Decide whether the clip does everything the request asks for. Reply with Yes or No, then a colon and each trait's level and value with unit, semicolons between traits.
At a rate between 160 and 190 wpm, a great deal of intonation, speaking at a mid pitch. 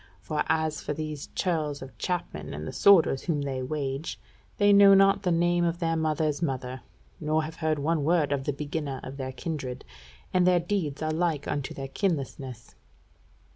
No: average, 180 wpm; average, 3.6 semitones; medium, 155 Hz